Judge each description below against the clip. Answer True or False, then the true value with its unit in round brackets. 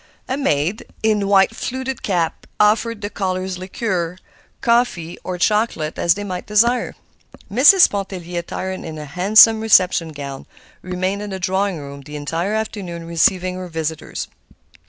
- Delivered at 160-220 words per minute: False (145 wpm)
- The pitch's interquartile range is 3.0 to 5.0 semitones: True (3.7 semitones)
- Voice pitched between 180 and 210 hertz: True (185 Hz)